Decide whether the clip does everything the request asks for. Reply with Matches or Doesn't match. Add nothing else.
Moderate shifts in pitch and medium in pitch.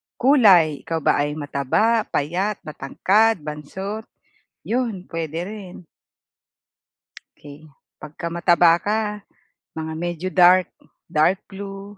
Matches